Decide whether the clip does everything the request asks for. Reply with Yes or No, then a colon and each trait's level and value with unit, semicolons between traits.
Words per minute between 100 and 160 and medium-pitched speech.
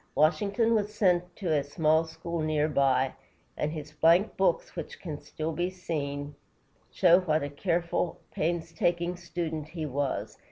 Yes: average, 150 wpm; medium, 165 Hz